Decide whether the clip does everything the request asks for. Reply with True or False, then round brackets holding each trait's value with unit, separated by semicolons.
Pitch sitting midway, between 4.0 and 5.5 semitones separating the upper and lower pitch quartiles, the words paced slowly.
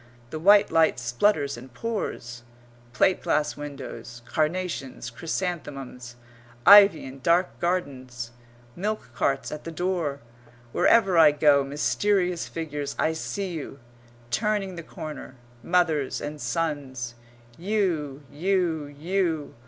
True (155 Hz; 4.7 semitones; 115 wpm)